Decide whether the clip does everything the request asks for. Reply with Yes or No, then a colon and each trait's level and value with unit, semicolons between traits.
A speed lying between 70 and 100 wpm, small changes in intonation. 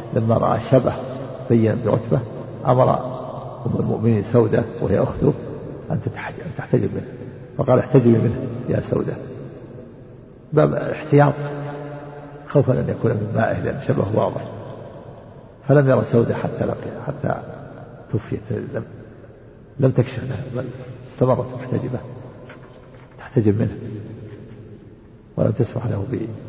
No: average, 110 wpm; narrow, 2.2 semitones